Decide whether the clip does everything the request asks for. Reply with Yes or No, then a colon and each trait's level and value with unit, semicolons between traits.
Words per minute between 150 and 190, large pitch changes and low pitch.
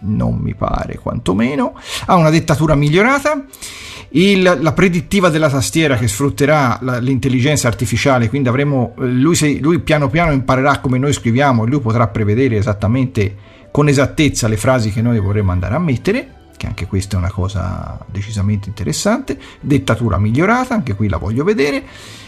Yes: average, 160 wpm; wide, 5.9 semitones; low, 130 Hz